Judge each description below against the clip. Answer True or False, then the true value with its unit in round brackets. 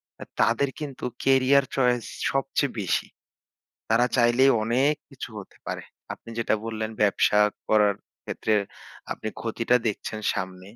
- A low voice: True (120 Hz)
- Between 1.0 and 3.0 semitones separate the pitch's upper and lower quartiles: False (3.7 semitones)